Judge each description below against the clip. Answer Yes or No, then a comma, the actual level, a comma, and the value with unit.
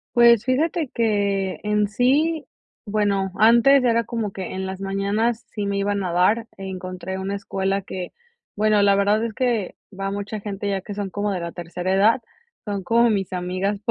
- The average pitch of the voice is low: No, high, 200 Hz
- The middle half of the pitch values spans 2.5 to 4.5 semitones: Yes, average, 2.9 semitones